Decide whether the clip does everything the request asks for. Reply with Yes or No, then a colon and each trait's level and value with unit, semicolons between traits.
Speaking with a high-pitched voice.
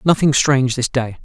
No: low, 130 Hz